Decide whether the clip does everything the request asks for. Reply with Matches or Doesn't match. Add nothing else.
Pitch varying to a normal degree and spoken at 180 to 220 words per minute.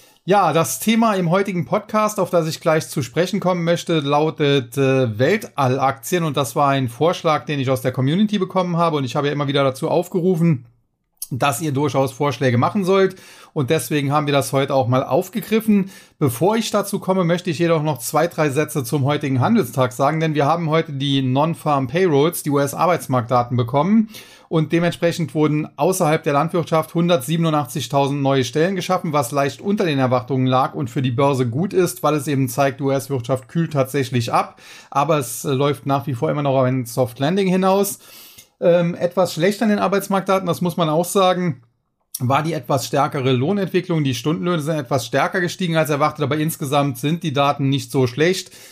Matches